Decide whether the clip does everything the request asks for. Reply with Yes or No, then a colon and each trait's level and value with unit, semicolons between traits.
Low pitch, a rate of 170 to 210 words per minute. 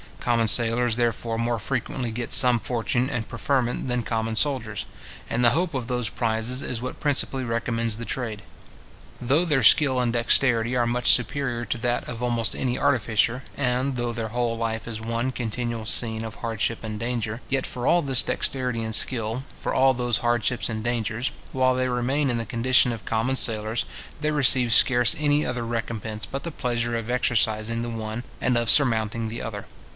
Yes: low, 120 Hz; average, 185 wpm